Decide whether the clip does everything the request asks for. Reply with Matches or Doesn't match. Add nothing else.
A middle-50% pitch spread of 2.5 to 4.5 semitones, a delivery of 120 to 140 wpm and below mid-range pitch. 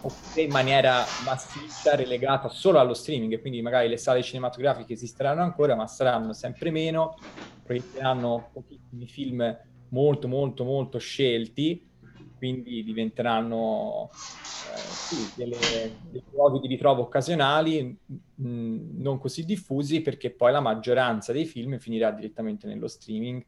Matches